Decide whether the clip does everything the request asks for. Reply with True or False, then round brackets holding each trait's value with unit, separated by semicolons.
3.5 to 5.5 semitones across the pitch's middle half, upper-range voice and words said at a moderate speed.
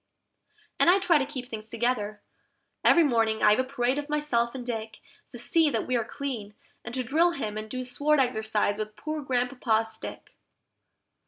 True (4.3 semitones; 245 Hz; 185 wpm)